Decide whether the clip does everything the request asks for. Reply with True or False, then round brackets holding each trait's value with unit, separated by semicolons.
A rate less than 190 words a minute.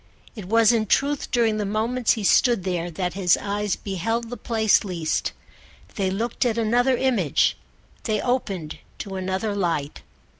True (155 wpm)